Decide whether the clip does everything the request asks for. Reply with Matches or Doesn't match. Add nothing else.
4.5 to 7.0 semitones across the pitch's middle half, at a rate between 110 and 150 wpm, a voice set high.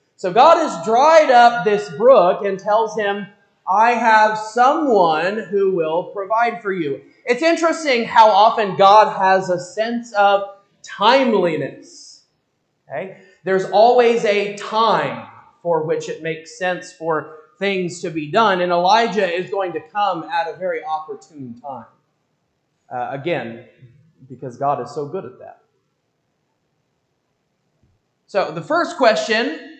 Matches